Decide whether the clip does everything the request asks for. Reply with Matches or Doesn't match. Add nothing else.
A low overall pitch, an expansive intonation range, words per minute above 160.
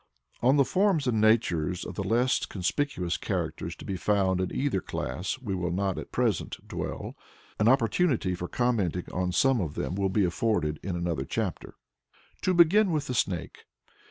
Matches